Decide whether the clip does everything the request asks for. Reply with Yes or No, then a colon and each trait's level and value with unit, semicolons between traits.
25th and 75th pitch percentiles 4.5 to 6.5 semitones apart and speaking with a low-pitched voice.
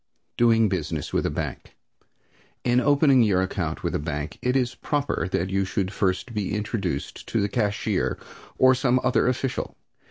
Yes: average, 5.2 semitones; low, 105 Hz